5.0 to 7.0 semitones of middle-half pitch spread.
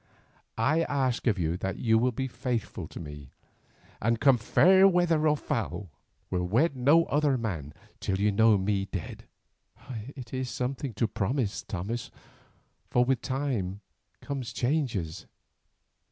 Yes: wide, 5.6 semitones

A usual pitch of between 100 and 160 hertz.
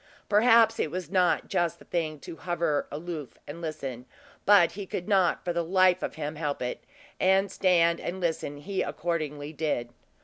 No: medium, 170 Hz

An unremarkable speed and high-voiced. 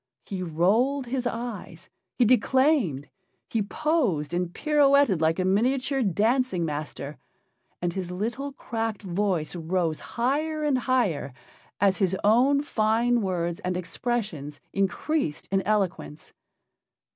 No: slow, 120 wpm; high, 210 Hz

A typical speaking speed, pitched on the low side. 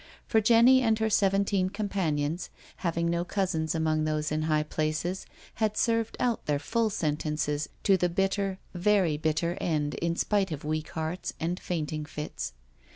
No: average, 160 wpm; medium, 170 Hz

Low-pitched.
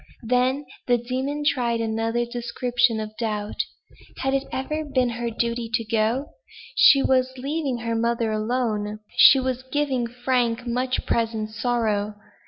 No: high, 240 Hz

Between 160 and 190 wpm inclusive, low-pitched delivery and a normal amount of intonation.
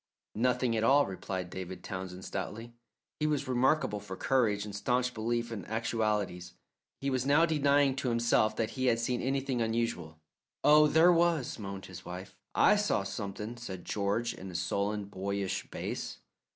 Yes: average, 165 wpm; low, 115 Hz; average, 4.9 semitones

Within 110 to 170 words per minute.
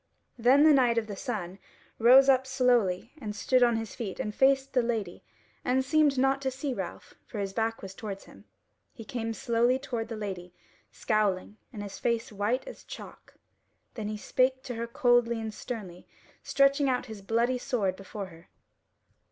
No: average, 180 wpm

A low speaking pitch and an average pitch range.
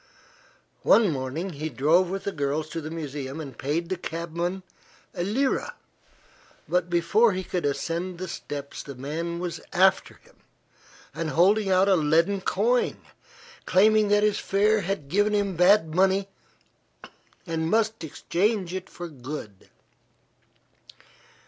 No: medium, 175 Hz; average, 3.8 semitones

